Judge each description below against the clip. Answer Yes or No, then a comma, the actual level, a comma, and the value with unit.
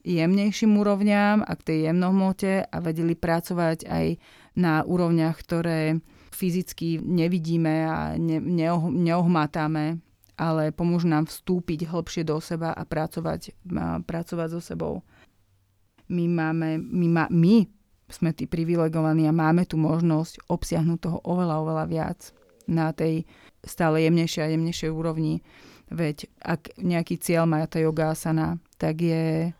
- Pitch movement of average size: No, narrow, 1.5 semitones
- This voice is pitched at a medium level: Yes, medium, 165 Hz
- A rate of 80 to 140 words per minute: Yes, average, 130 wpm